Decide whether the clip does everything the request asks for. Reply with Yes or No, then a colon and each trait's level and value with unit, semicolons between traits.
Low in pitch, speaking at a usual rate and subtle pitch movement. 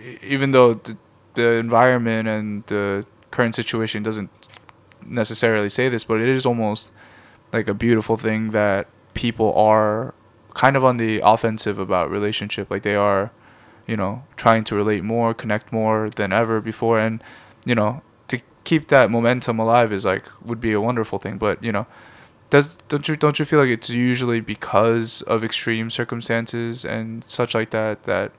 Yes: low, 110 Hz; average, 170 wpm; narrow, 1.8 semitones